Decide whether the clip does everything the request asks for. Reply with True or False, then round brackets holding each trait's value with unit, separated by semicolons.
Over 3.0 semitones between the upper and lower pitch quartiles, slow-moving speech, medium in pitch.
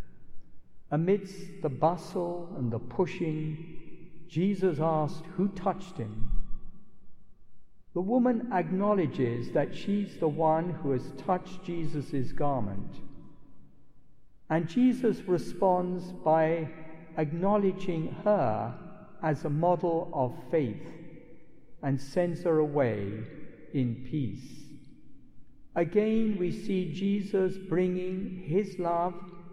True (3.9 semitones; 95 wpm; 170 Hz)